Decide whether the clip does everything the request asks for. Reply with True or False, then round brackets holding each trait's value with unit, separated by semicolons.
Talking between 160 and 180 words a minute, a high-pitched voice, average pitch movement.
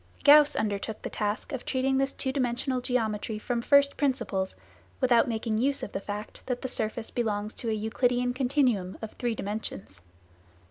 True (170 wpm; 240 Hz; 3.4 semitones)